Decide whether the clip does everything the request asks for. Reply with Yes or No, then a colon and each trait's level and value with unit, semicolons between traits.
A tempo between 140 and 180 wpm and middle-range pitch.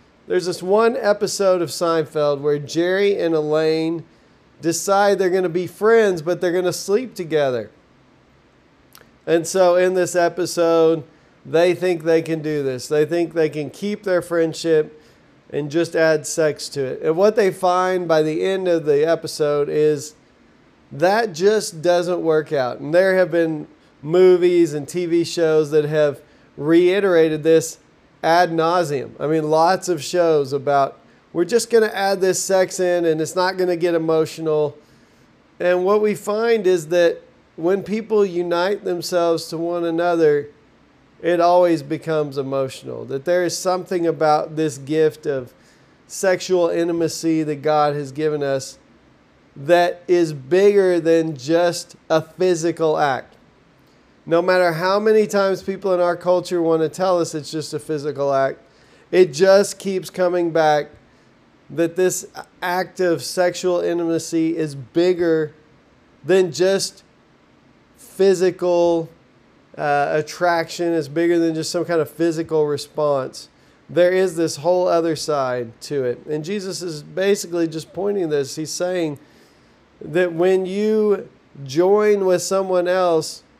Yes: average, 150 wpm; medium, 170 Hz